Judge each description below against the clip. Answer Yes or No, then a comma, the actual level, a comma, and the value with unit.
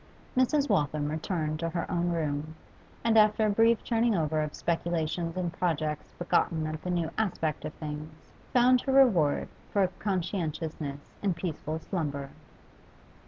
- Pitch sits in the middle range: Yes, medium, 165 Hz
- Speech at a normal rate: Yes, average, 145 wpm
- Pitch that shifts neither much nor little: Yes, average, 4.6 semitones